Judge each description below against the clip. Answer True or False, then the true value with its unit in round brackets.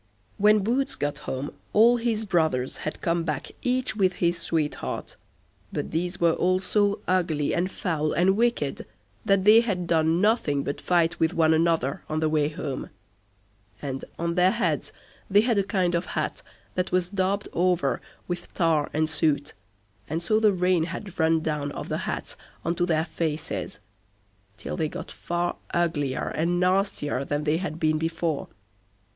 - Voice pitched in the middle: True (170 Hz)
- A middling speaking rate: True (170 wpm)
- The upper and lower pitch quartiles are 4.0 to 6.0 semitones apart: False (3.2 semitones)